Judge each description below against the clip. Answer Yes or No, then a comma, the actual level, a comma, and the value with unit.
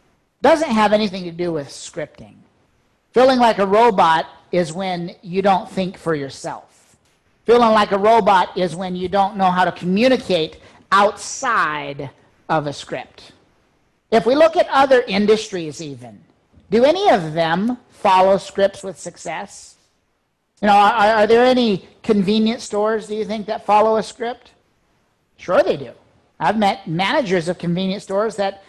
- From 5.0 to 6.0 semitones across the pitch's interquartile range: No, average, 3.8 semitones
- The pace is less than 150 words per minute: No, average, 155 wpm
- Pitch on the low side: No, high, 200 Hz